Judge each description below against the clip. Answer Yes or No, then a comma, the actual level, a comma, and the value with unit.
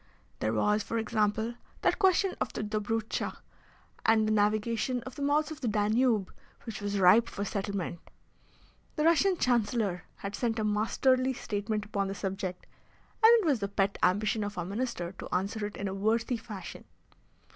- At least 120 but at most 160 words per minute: No, average, 170 wpm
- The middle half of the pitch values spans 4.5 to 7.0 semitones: No, average, 2.9 semitones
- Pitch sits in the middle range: No, high, 215 Hz